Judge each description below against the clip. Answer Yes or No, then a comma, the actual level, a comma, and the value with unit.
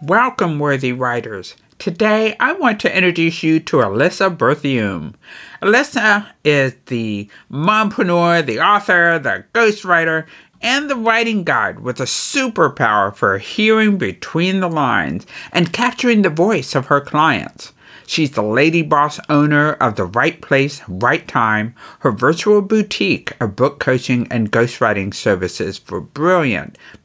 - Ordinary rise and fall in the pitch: No, wide, 7.9 semitones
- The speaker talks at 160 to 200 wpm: No, slow, 135 wpm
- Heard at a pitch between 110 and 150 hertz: No, medium, 165 Hz